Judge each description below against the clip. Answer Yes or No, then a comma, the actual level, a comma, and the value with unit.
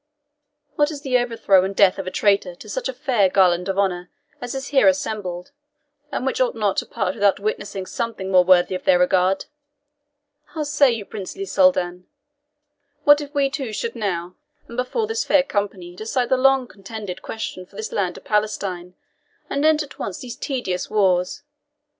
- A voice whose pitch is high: Yes, high, 210 Hz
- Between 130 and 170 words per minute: No, average, 185 wpm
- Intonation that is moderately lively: No, wide, 6.4 semitones